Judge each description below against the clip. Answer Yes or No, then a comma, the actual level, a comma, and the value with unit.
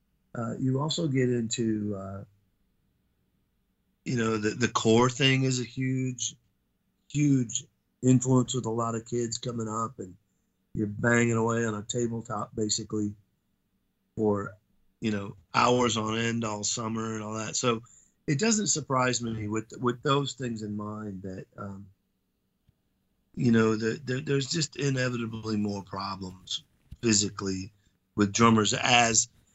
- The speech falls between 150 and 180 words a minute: No, average, 140 wpm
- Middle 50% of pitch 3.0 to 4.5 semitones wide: Yes, average, 3.3 semitones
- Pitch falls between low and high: No, low, 115 Hz